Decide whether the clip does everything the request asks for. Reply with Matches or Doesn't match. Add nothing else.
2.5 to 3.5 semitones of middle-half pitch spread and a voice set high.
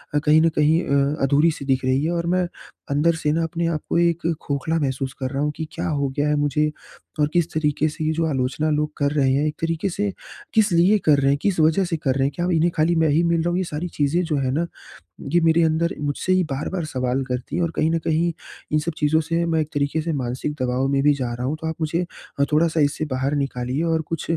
Doesn't match